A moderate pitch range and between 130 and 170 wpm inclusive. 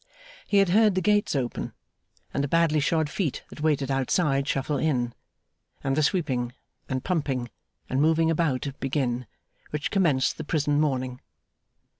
Yes: average, 3.8 semitones; average, 150 wpm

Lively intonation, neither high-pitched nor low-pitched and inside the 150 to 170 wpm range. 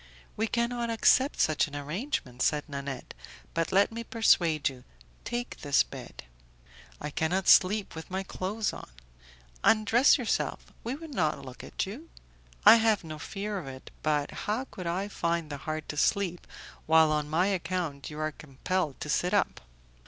Yes: wide, 6.1 semitones; medium, 175 Hz; average, 165 wpm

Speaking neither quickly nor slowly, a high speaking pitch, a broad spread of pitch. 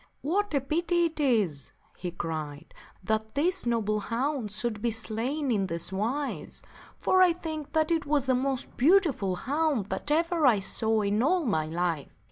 Yes: average, 175 wpm; high, 245 Hz; wide, 7.0 semitones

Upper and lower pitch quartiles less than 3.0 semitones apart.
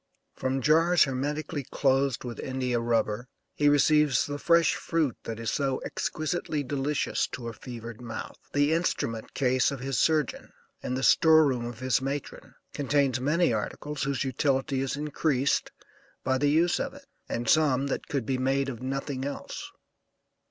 Yes: narrow, 2.6 semitones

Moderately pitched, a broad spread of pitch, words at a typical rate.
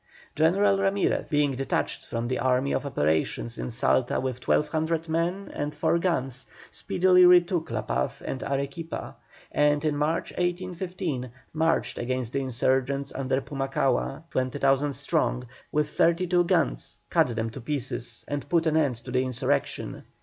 No: medium, 145 Hz; average, 4.5 semitones; average, 150 wpm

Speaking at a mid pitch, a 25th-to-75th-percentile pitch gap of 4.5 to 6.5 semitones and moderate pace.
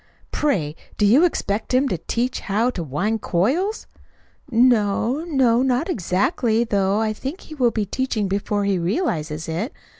No: high, 225 Hz; average, 4.9 semitones; average, 155 wpm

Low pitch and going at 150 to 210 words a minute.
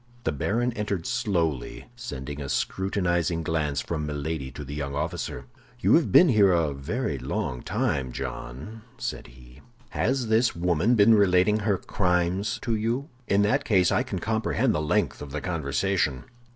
Yes: very low, 90 Hz; average, 165 wpm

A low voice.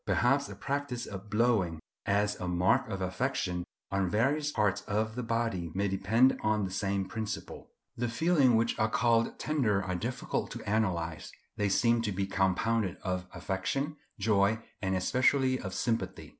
Yes: low, 105 Hz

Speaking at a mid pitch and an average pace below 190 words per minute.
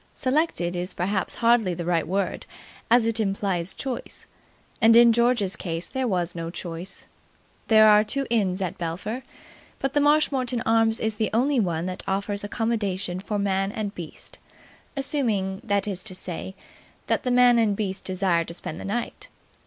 No: high, 205 Hz; average, 170 wpm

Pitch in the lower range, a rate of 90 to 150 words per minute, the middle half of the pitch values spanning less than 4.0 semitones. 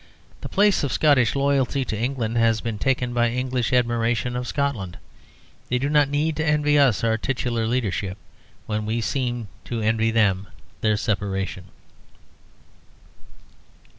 Yes: low, 120 Hz; average, 140 wpm; average, 3.5 semitones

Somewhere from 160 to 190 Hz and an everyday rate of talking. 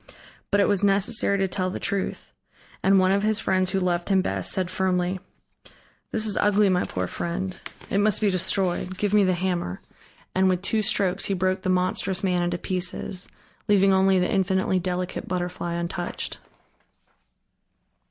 Yes: medium, 185 Hz; average, 170 wpm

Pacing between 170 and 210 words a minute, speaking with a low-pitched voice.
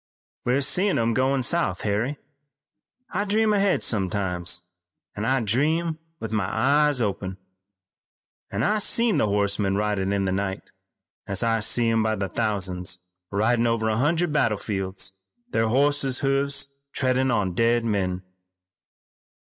No: average, 140 wpm; low, 115 Hz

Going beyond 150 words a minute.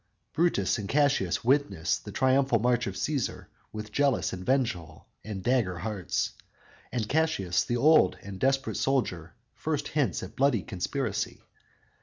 No: slow, 135 wpm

